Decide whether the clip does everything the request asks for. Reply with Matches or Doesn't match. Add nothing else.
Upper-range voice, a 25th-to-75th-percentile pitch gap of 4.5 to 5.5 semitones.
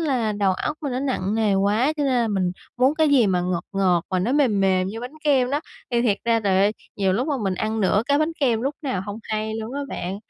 Matches